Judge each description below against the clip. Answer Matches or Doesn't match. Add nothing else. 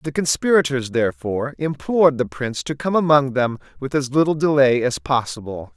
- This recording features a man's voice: Matches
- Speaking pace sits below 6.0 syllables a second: Matches